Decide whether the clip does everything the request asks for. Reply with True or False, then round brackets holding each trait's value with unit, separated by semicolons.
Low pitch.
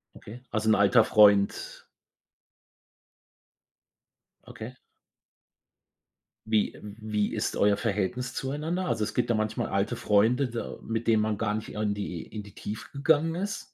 True (110 Hz)